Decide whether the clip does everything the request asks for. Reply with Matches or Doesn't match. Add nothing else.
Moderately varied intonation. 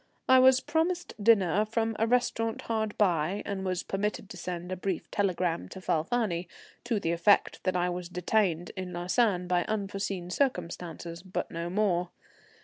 Matches